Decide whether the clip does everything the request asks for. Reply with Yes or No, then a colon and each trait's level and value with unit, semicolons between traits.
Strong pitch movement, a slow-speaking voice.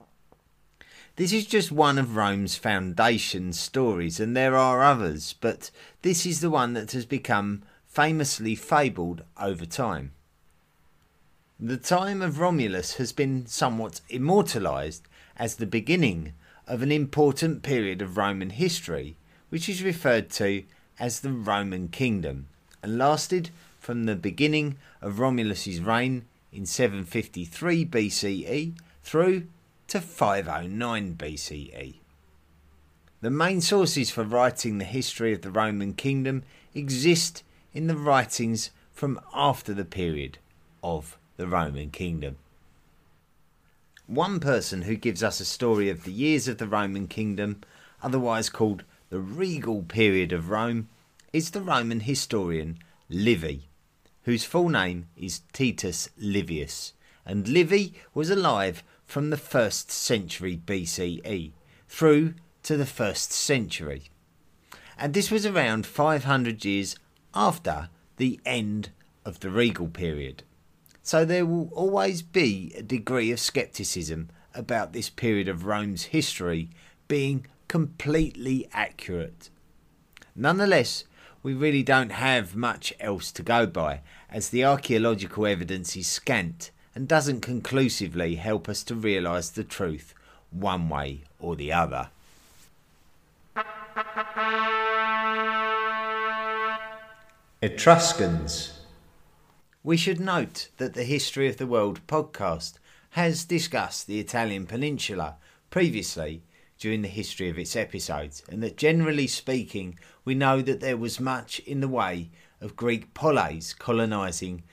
Yes: wide, 8.3 semitones; slow, 125 wpm